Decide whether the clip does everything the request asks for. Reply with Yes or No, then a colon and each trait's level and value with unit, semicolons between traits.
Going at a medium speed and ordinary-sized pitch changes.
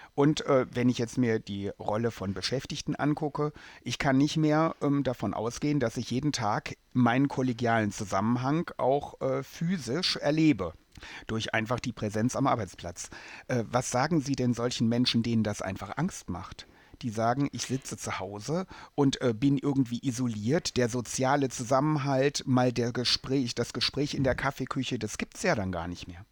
Yes: average, 175 wpm; average, 3.7 semitones